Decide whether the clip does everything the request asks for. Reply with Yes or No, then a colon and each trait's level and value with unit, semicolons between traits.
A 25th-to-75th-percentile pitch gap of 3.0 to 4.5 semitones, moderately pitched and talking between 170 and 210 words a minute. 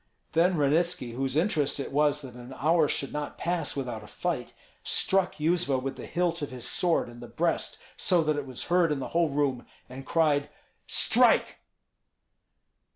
Yes: average, 4.0 semitones; medium, 150 Hz; average, 175 wpm